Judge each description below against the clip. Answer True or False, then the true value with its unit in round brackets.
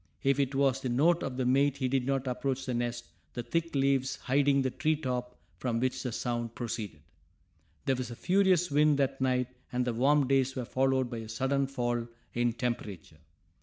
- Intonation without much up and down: True (2.2 semitones)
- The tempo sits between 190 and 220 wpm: True (200 wpm)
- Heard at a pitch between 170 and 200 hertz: False (130 Hz)